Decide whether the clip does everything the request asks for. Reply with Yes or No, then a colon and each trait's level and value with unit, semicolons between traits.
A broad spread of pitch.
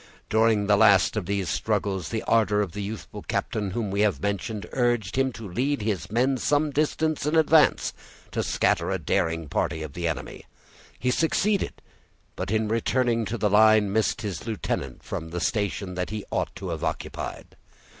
No: average, 3.4 semitones